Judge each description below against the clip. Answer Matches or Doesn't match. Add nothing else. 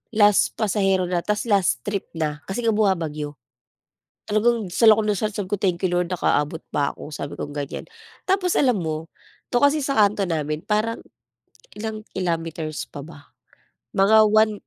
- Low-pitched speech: Doesn't match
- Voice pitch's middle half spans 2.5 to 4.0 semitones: Doesn't match